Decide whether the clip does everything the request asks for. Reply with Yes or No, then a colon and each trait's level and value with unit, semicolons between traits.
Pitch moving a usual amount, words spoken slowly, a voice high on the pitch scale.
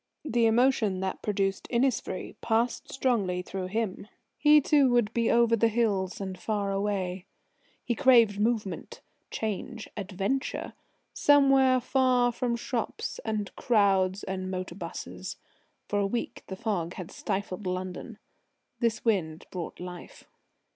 Yes: average, 4.0 semitones; slow, 130 wpm; high, 210 Hz